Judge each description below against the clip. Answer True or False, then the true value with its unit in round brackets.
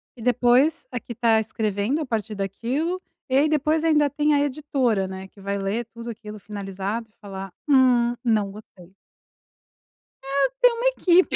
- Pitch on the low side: False (235 Hz)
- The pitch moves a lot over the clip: True (5.9 semitones)